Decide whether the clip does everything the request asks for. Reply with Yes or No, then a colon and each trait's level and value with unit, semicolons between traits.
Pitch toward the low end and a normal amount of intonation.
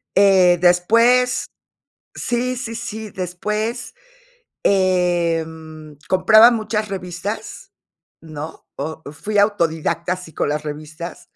No: medium, 185 Hz; average, 4.9 semitones